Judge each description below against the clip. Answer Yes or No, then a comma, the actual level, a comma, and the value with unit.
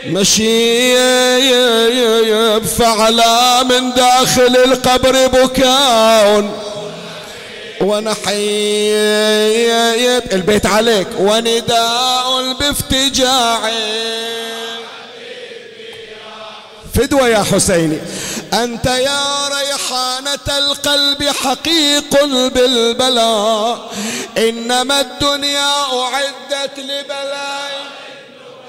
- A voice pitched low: No, high, 245 Hz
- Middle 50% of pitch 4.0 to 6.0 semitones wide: No, average, 3.5 semitones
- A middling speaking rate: No, slow, 50 wpm